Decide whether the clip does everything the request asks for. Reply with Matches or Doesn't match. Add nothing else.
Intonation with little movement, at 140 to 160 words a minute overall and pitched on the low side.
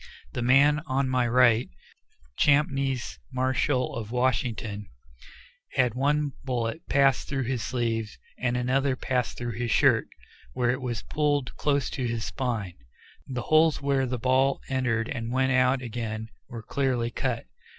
Matches